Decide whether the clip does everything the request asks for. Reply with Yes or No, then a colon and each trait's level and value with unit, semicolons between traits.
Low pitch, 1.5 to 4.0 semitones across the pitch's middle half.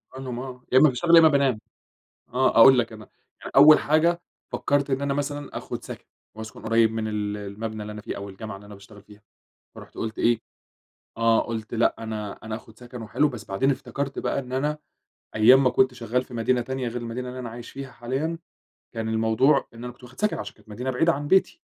Yes: low, 120 Hz; average, 3.5 semitones